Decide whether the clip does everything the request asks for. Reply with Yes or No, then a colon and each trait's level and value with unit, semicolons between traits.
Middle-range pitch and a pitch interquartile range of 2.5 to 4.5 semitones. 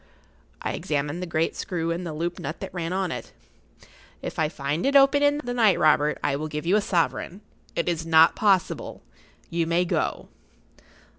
Yes: medium, 170 Hz; average, 3.5 semitones